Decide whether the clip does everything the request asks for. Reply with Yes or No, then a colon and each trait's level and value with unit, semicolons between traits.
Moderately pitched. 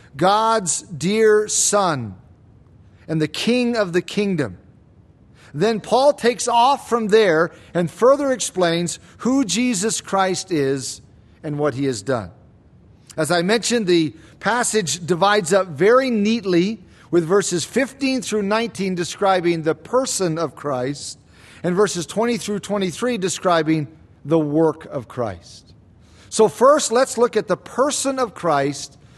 Yes: medium, 180 Hz